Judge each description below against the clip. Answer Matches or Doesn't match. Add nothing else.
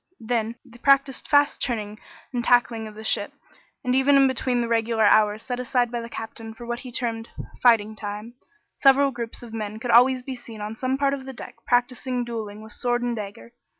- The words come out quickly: Matches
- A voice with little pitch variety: Matches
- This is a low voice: Doesn't match